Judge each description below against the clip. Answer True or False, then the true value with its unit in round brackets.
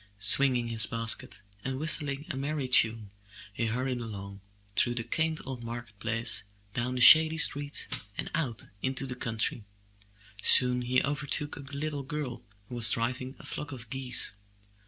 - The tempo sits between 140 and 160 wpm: True (155 wpm)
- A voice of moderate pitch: False (125 Hz)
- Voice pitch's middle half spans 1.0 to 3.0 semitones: False (3.4 semitones)